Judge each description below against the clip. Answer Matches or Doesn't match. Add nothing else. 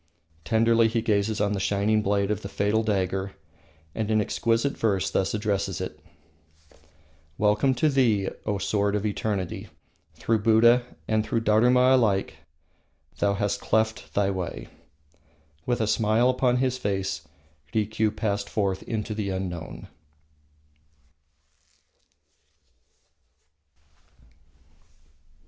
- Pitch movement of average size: Doesn't match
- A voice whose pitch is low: Matches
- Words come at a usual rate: Doesn't match